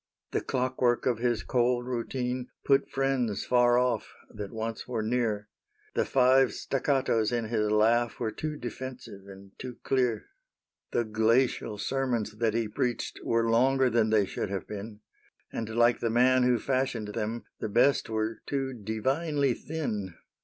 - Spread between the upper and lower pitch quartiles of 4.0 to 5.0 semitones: No, average, 2.8 semitones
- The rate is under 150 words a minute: No, average, 155 wpm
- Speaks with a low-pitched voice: Yes, low, 120 Hz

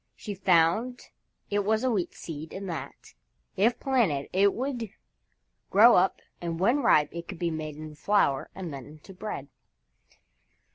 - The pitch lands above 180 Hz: Yes, high, 190 Hz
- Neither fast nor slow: Yes, average, 155 wpm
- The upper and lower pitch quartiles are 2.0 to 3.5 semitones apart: No, average, 5.3 semitones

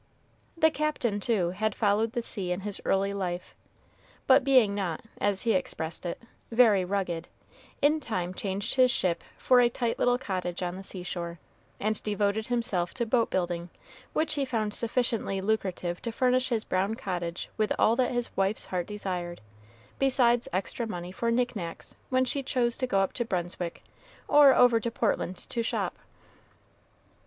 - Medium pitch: No, high, 210 Hz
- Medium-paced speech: Yes, average, 165 wpm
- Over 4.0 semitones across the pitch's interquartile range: Yes, average, 4.8 semitones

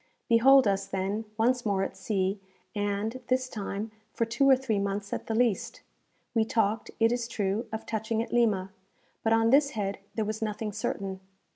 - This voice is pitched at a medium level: No, high, 220 Hz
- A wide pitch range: No, average, 2.7 semitones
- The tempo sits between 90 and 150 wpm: No, average, 180 wpm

